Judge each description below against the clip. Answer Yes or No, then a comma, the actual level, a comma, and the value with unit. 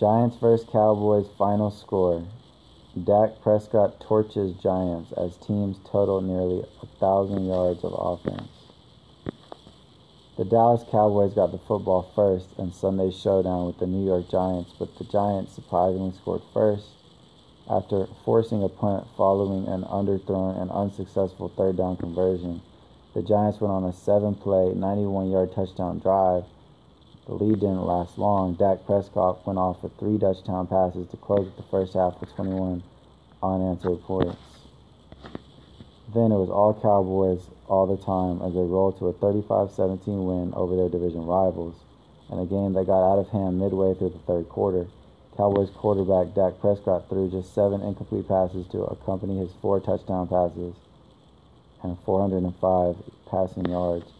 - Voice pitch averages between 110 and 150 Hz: No, very low, 95 Hz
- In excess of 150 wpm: No, average, 145 wpm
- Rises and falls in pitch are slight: Yes, narrow, 1.9 semitones